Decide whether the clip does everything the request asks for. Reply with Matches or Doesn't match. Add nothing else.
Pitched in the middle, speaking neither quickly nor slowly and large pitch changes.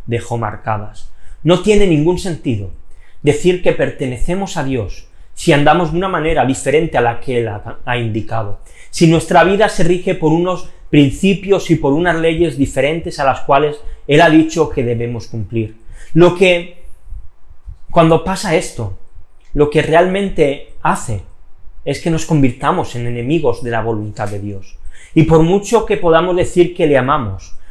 Matches